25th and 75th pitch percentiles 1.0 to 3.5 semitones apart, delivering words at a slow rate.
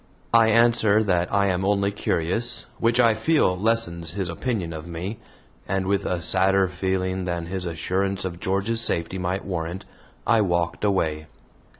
No: average, 3.2 semitones; average, 160 wpm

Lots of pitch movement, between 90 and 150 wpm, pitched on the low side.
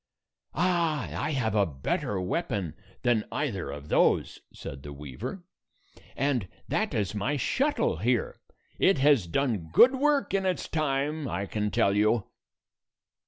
Yes: wide, 8.5 semitones; average, 145 wpm; low, 125 Hz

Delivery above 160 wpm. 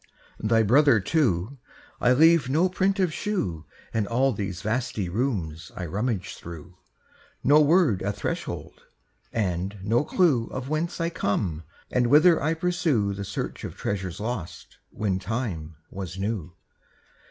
No: average, 140 wpm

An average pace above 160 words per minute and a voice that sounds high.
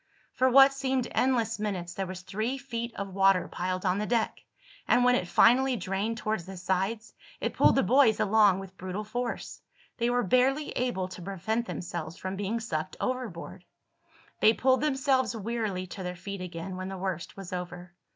Yes: average, 180 wpm; high, 205 Hz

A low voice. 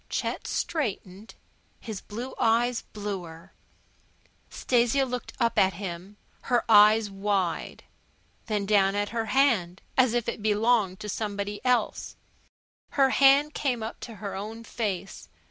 No: high, 215 Hz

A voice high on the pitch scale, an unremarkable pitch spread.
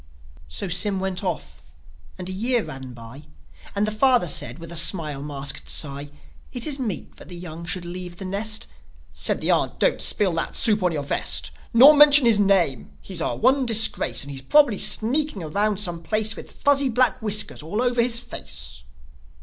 No: high, 195 Hz; wide, 6.1 semitones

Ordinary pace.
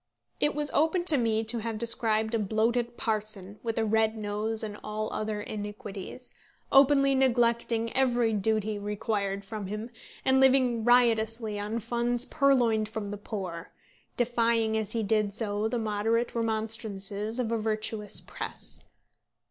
Yes: average, 150 wpm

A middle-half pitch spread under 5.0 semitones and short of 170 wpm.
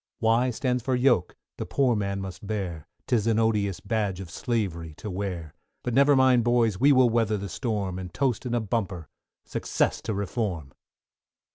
No: average, 4.2 semitones; average, 175 wpm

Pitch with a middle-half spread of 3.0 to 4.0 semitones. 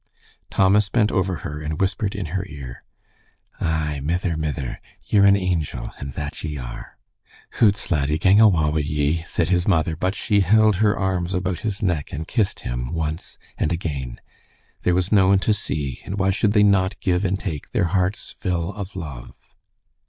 No: average, 4.5 semitones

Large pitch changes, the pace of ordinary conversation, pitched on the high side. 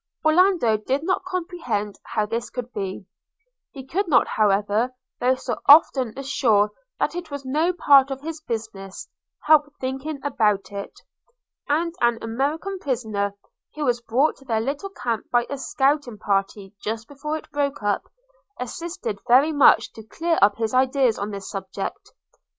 Yes: wide, 5.8 semitones; average, 160 wpm; very high, 260 Hz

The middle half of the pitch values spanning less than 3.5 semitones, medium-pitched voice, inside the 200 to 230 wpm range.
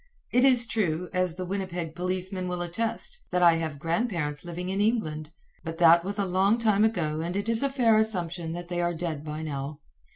No: average, 3.9 semitones; medium, 180 Hz; fast, 205 wpm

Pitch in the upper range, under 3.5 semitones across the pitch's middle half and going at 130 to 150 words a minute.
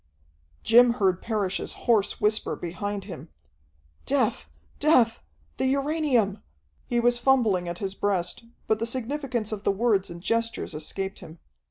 No: high, 215 Hz; average, 3.9 semitones; average, 140 wpm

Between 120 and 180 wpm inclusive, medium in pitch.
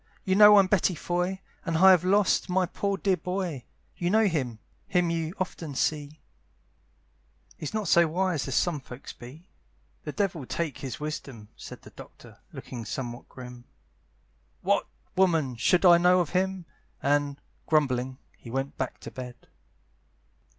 Yes: average, 155 wpm; medium, 165 Hz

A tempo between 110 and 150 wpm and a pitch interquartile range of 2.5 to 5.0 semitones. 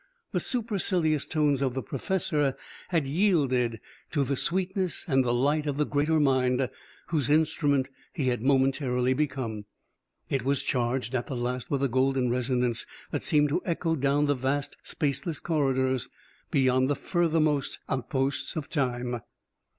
Yes: average, 145 wpm; average, 3.0 semitones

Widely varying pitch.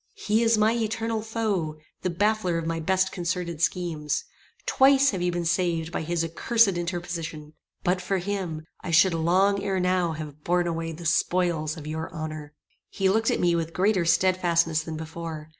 No: average, 2.9 semitones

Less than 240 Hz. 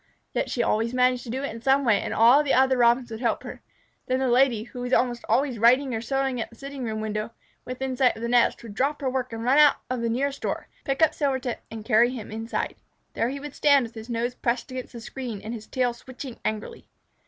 No: high, 245 Hz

